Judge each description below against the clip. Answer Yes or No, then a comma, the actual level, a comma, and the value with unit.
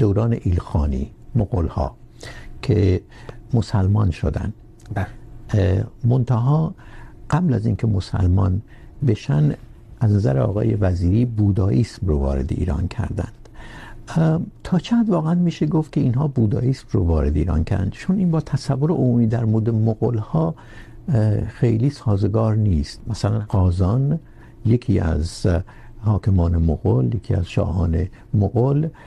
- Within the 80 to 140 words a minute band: Yes, average, 115 wpm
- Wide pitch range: No, average, 3.9 semitones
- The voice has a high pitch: No, low, 110 Hz